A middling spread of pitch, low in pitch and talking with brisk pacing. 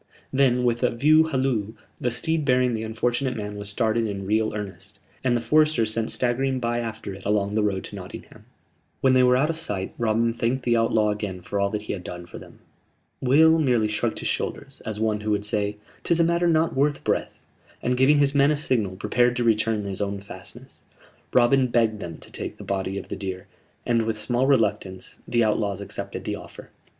Yes: average, 3.8 semitones; low, 115 Hz; fast, 215 wpm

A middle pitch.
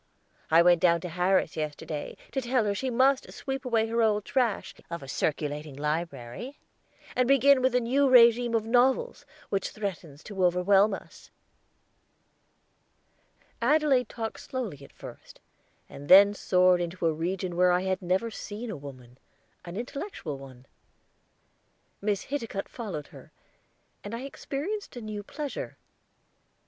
No: high, 205 Hz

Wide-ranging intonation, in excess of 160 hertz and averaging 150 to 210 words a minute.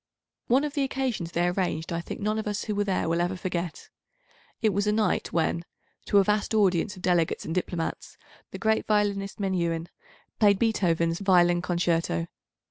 No: average, 3.5 semitones; medium, 185 Hz; average, 180 wpm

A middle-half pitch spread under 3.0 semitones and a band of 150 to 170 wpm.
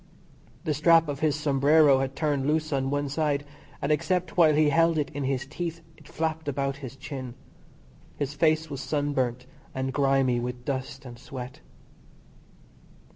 Yes: narrow, 2.6 semitones; average, 160 wpm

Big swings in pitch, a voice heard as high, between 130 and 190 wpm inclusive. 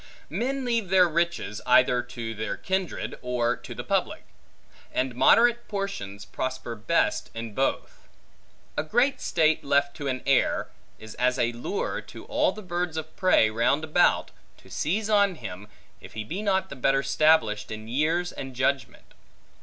No: wide, 7.5 semitones; medium, 140 Hz; average, 160 wpm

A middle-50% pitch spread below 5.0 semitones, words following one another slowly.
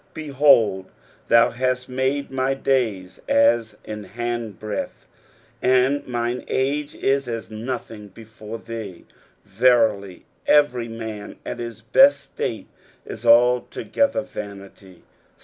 Yes: average, 3.4 semitones; slow, 100 wpm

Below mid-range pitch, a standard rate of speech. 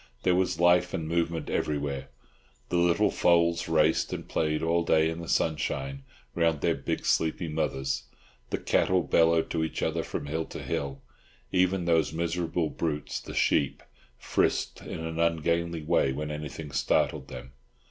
Yes: very low, 80 Hz; average, 155 wpm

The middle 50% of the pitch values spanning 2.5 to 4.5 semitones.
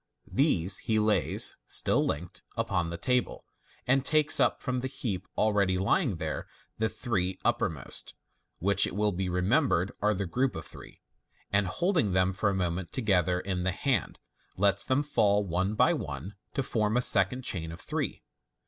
No: average, 5.0 semitones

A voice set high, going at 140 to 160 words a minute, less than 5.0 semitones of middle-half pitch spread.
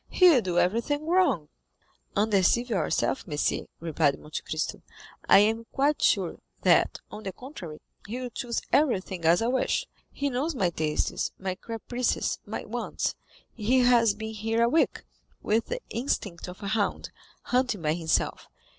No: high, 220 Hz; average, 155 wpm; wide, 5.6 semitones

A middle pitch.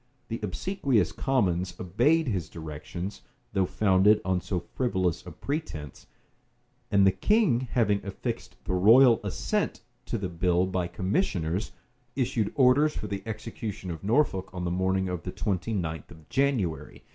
No: very low, 95 Hz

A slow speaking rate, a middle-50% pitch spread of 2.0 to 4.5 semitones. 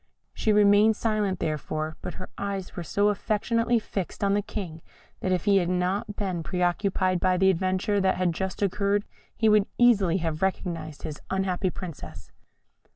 No: average, 170 wpm; narrow, 2.5 semitones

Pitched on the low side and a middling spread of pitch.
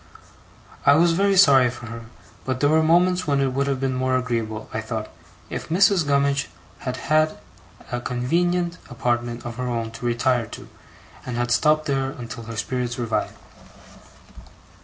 Yes: low, 130 Hz; average, 4.3 semitones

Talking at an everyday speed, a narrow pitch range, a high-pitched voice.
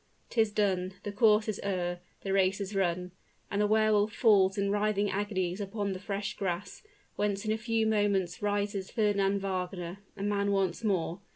Yes: average, 180 wpm; narrow, 1.6 semitones; high, 200 Hz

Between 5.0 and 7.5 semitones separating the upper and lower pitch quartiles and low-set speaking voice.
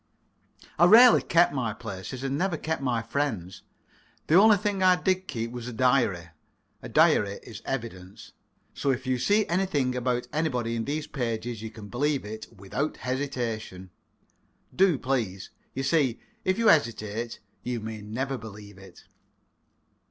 Yes: average, 5.3 semitones; low, 125 Hz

